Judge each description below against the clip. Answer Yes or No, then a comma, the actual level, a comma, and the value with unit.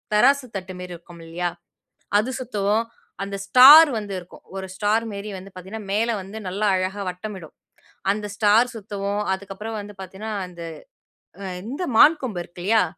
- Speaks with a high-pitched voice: Yes, high, 205 Hz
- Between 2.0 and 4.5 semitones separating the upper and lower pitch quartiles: Yes, average, 2.9 semitones